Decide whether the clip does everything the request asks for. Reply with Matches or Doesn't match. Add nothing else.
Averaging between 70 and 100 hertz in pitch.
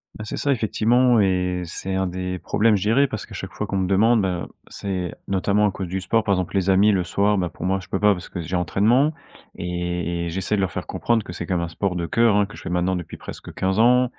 Matches